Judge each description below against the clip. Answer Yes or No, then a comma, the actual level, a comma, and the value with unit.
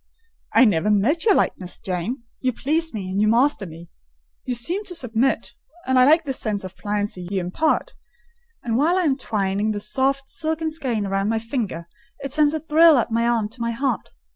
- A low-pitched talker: No, high, 235 Hz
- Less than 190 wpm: No, average, 195 wpm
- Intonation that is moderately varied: No, wide, 6.2 semitones